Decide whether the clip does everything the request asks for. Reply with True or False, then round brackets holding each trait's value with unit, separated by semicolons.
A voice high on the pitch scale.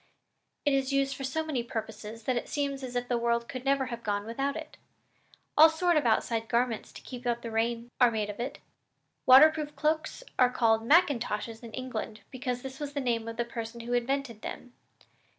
True (245 Hz)